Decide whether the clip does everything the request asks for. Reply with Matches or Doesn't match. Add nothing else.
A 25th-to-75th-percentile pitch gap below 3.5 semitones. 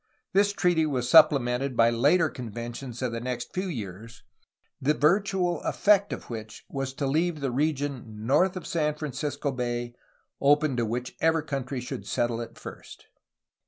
Doesn't match